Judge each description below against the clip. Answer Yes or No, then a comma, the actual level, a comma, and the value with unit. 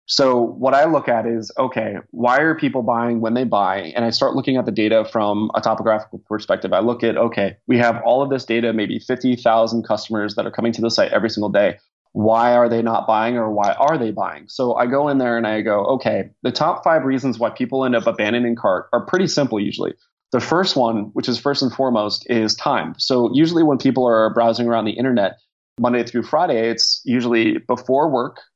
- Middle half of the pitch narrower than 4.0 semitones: Yes, narrow, 2.4 semitones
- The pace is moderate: No, fast, 225 wpm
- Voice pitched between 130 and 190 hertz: No, low, 115 Hz